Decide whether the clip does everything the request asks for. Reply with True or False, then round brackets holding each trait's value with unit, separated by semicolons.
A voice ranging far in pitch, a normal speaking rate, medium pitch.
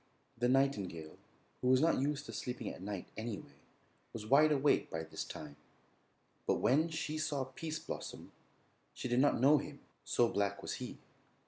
False (5.7 semitones; 165 wpm; 130 Hz)